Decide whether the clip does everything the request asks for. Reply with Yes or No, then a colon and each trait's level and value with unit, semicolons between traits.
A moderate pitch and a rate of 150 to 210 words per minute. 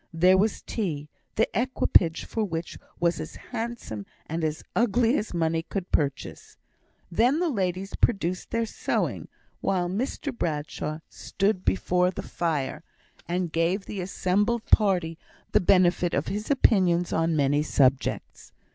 No: medium, 180 Hz; average, 140 wpm